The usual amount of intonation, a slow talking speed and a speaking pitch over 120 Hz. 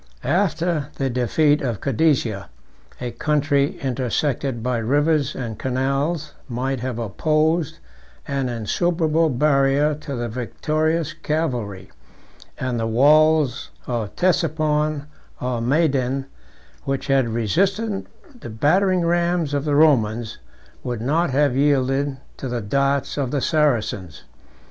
Yes: average, 3.9 semitones; slow, 115 wpm; medium, 140 Hz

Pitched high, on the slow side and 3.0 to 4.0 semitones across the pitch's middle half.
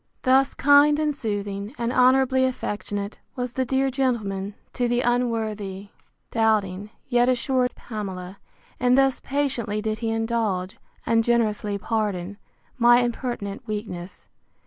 Yes: high, 230 Hz; slow, 125 wpm; average, 3.6 semitones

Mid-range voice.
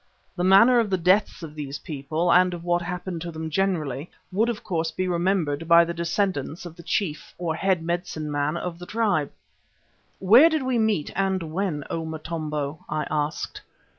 Yes: medium, 170 Hz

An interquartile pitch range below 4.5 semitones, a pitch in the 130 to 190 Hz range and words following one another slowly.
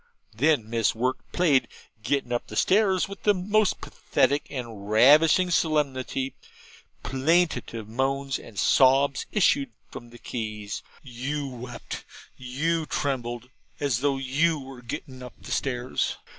Yes: average, 3.7 semitones; low, 135 Hz; slow, 120 wpm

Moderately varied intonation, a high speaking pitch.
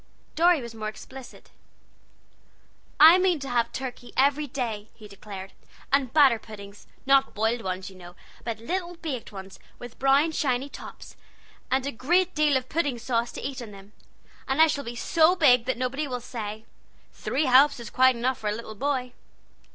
Yes: average, 4.2 semitones; very high, 255 Hz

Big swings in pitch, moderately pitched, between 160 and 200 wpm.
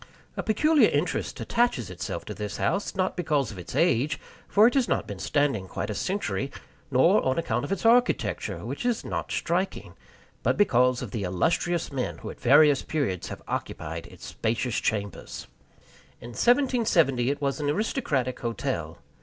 Yes: wide, 8.6 semitones; medium, 145 Hz; average, 170 wpm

